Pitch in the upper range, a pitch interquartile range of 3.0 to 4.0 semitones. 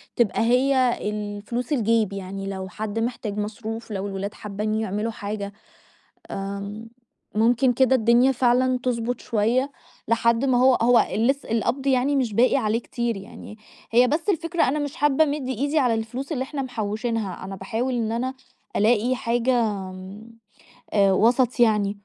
Yes: high, 230 Hz; average, 3.4 semitones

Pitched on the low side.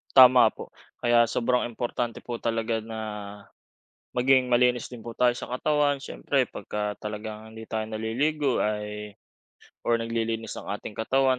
Yes: low, 115 Hz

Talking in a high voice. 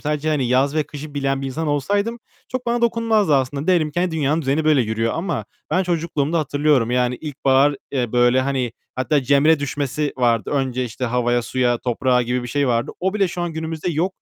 No: medium, 145 Hz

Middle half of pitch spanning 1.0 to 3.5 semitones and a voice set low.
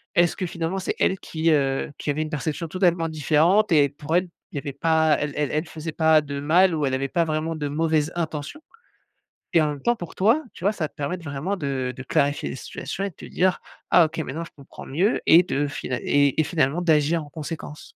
No: average, 2.9 semitones; medium, 155 Hz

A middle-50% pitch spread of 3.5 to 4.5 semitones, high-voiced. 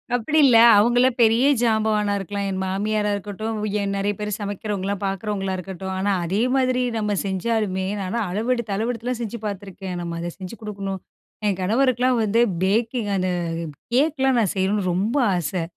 No: average, 3.1 semitones; high, 210 Hz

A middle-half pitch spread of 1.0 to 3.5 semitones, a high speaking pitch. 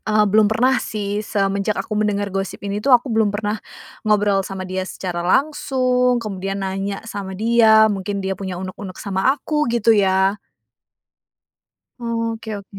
Yes: narrow, 2.6 semitones; high, 205 Hz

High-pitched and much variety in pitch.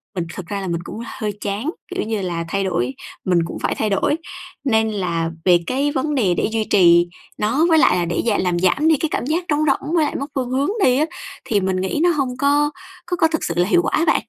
Yes: high, 220 Hz; wide, 8.0 semitones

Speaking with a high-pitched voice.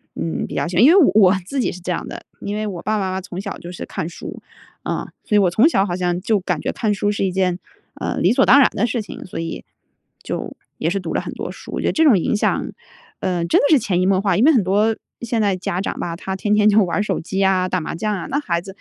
Yes: high, 195 Hz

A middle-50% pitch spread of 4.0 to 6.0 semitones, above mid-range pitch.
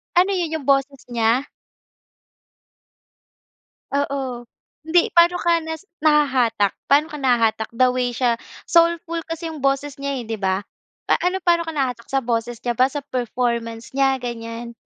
Yes: average, 4.7 semitones; very high, 265 Hz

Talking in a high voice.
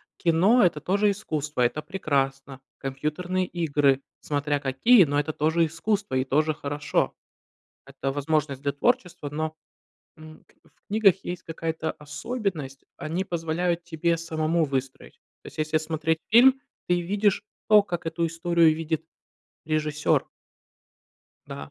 No: medium, 160 Hz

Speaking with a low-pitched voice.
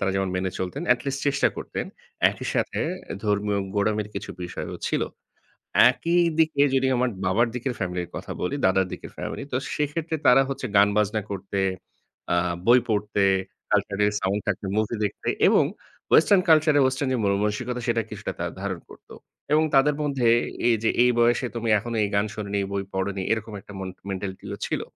Yes: low, 105 Hz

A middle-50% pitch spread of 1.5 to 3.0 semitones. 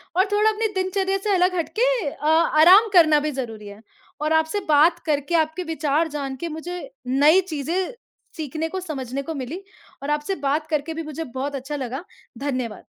No: average, 4.0 semitones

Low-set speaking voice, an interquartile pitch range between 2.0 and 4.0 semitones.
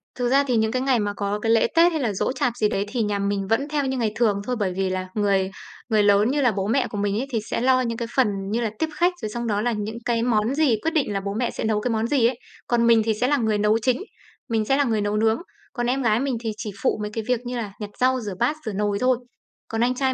No: high, 230 Hz; average, 3.3 semitones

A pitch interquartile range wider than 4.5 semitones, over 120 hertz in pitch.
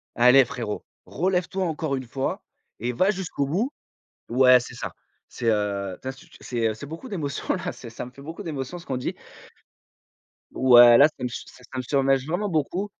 Yes: average, 5.0 semitones; low, 135 Hz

